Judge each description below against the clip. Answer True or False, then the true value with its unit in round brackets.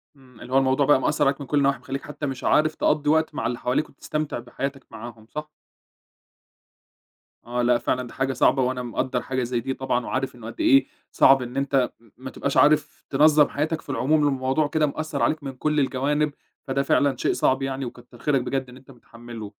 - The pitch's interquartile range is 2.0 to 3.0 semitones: True (2.7 semitones)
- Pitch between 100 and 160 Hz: True (135 Hz)